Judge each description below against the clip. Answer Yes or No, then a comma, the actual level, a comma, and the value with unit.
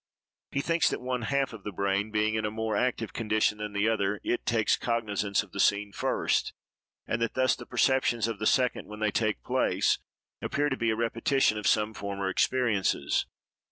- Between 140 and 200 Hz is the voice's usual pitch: No, low, 110 Hz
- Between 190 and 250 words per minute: Yes, average, 195 wpm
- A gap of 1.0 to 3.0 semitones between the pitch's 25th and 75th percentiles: Yes, narrow, 2.5 semitones